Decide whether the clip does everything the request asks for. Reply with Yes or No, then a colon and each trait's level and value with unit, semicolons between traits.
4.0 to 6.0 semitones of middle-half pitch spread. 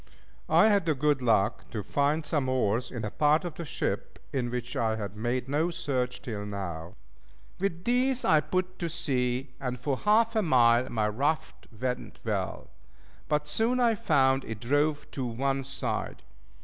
Yes: average, 4.9 semitones